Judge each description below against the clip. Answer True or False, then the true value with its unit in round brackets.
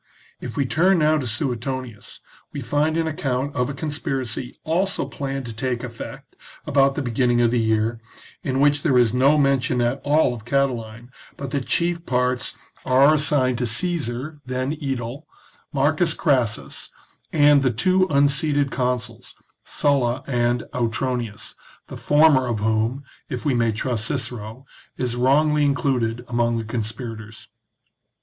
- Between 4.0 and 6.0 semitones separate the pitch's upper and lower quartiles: False (3.3 semitones)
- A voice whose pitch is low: True (130 Hz)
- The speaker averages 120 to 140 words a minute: False (150 wpm)